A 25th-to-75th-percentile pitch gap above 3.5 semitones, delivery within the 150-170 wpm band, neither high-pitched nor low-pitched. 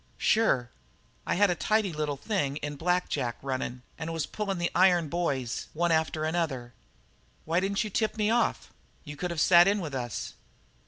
No: average, 5.1 semitones; average, 190 wpm; medium, 165 Hz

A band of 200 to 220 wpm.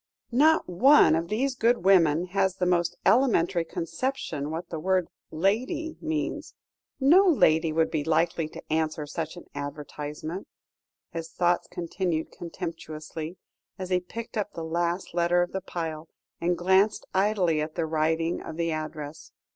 No: average, 150 wpm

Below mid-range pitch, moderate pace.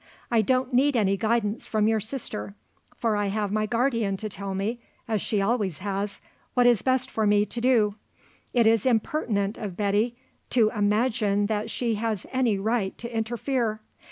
No: high, 220 Hz; average, 175 wpm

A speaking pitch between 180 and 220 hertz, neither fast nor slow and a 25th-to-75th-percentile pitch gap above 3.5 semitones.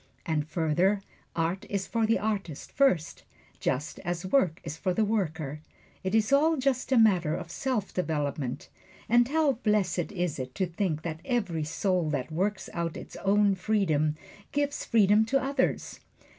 Yes: high, 190 Hz; average, 160 wpm; wide, 5.5 semitones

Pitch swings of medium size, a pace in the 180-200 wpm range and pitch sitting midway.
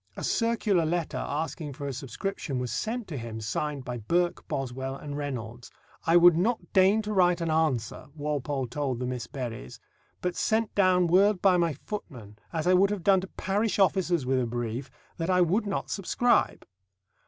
No: wide, 6.4 semitones; average, 185 wpm; medium, 160 Hz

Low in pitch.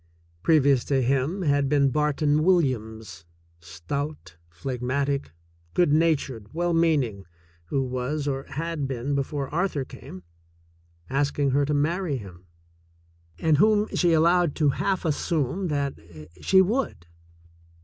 No: medium, 145 Hz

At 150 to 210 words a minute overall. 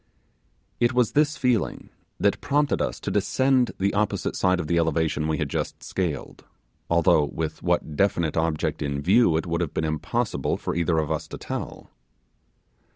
Yes: average, 170 wpm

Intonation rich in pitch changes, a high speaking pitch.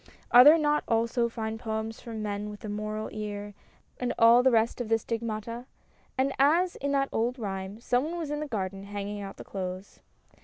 No: average, 3.2 semitones; high, 225 Hz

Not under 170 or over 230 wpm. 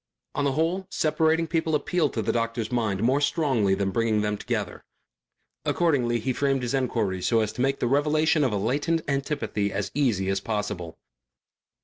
Yes: average, 175 wpm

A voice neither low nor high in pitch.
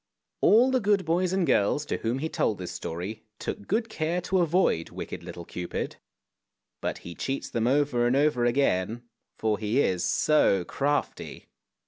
No: low, 130 Hz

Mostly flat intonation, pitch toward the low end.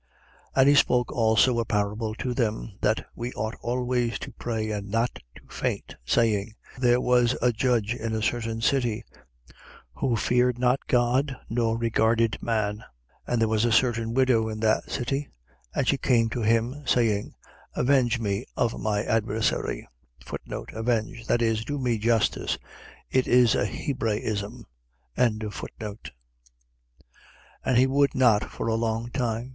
Yes: narrow, 2.1 semitones; low, 115 Hz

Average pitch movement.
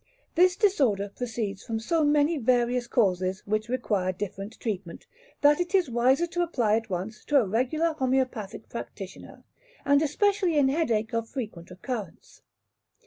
No: wide, 5.9 semitones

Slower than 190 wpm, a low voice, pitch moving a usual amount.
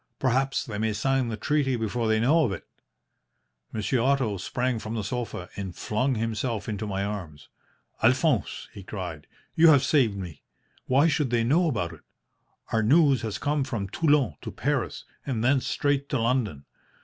Yes: average, 175 wpm; low, 115 Hz; average, 4.5 semitones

